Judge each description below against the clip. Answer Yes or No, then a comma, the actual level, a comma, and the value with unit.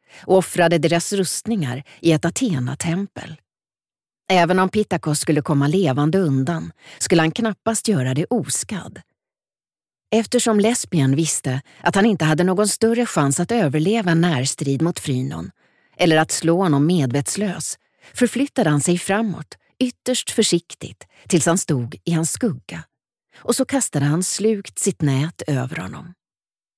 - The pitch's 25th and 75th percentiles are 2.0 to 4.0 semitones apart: No, wide, 5.6 semitones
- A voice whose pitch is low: No, medium, 170 Hz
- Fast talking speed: No, average, 140 wpm